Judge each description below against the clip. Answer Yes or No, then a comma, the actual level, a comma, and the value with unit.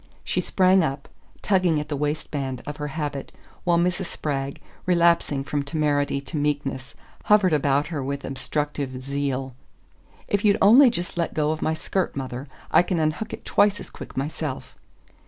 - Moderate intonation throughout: Yes, average, 3.7 semitones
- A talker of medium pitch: Yes, medium, 150 Hz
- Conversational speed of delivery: Yes, average, 165 wpm